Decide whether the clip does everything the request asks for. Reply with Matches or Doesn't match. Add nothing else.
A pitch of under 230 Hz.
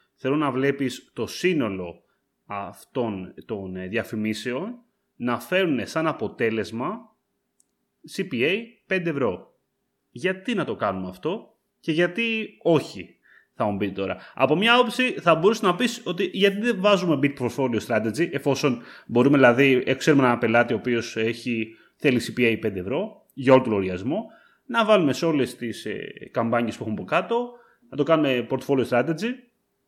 Matches